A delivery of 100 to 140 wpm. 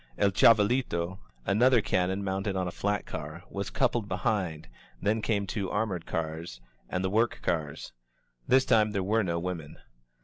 No: average, 165 wpm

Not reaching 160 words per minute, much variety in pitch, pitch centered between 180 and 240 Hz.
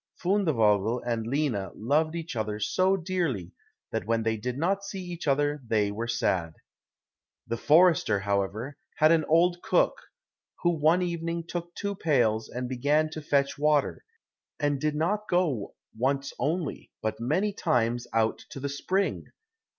No: average, 150 wpm; wide, 6.8 semitones; medium, 145 Hz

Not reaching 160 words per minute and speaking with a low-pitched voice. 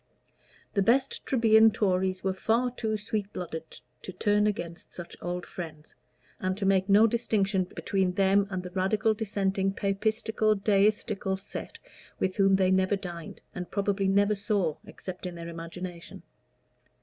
No: average, 150 wpm; high, 195 Hz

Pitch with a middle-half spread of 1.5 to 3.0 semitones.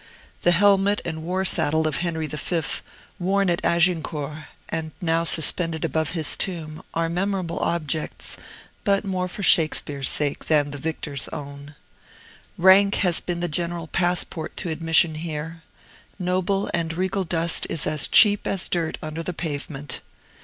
Yes: narrow, 2.6 semitones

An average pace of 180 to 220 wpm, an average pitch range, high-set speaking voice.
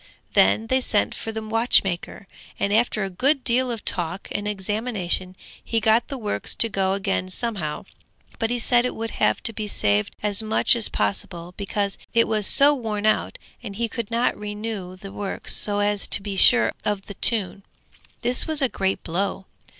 Yes: average, 190 wpm; average, 3.0 semitones; high, 210 Hz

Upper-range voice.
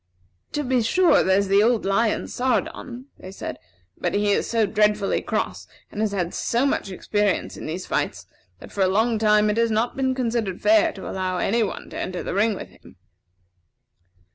Yes: high, 215 Hz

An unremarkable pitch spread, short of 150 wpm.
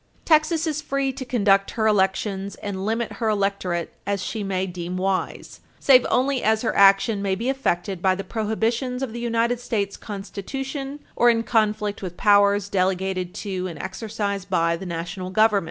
No: average, 3.7 semitones; average, 170 wpm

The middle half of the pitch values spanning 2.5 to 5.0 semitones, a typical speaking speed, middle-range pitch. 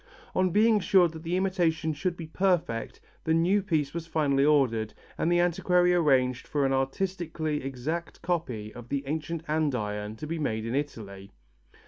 Yes: average, 4.6 semitones; average, 165 wpm; medium, 155 Hz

